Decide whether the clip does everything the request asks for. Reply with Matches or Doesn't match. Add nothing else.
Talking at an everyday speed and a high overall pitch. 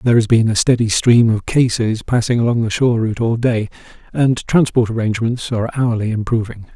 Doesn't match